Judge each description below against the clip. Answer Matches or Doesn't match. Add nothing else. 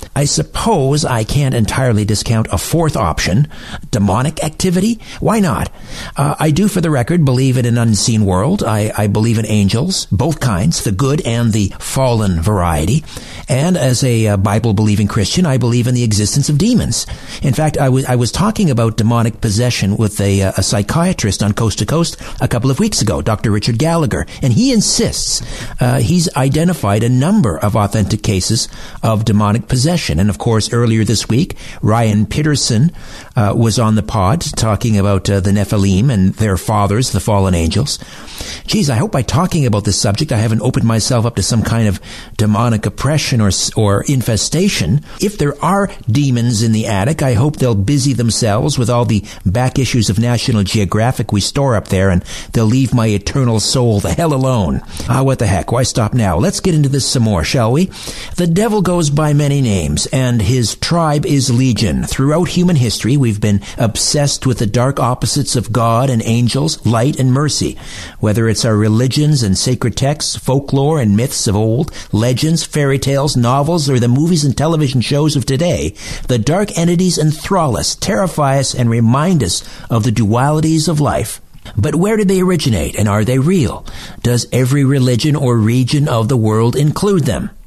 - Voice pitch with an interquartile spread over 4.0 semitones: Matches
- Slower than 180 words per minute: Doesn't match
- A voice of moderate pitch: Doesn't match